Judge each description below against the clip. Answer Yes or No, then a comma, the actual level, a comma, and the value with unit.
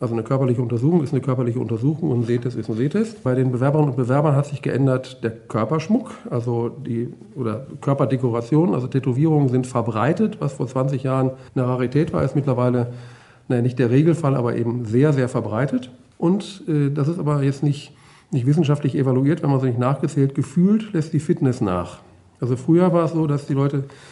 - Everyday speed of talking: No, fast, 195 wpm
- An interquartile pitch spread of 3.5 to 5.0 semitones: No, average, 3.1 semitones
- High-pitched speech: No, low, 135 Hz